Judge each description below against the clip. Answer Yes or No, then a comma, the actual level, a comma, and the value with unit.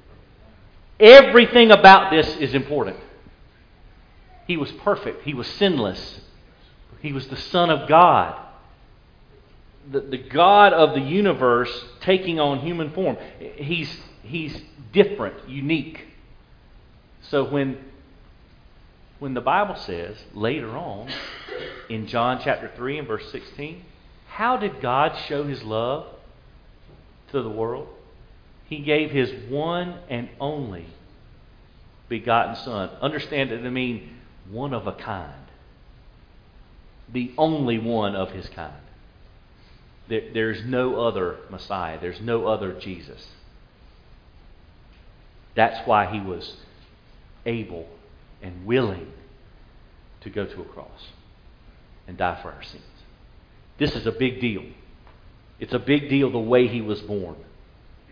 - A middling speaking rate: No, slow, 120 wpm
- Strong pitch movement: Yes, wide, 6.3 semitones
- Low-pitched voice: Yes, low, 120 Hz